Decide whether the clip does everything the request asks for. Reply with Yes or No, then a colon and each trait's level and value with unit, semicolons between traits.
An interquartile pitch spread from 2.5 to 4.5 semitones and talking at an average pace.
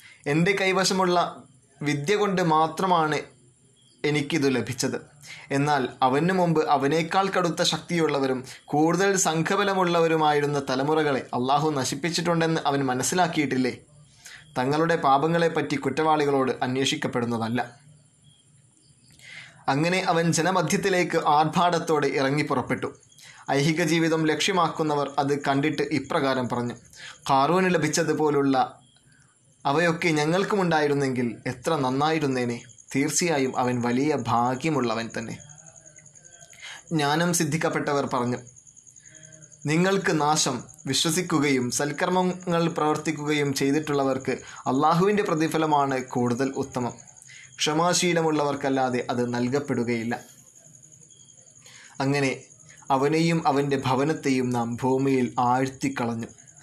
Yes: average, 3.5 semitones; average, 75 wpm